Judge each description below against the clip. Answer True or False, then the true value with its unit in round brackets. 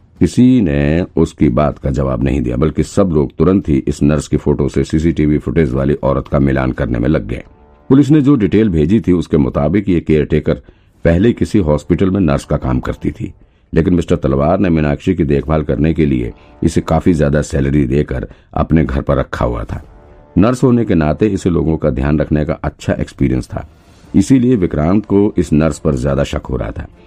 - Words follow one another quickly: True (200 wpm)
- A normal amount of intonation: True (3.9 semitones)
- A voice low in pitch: True (75 Hz)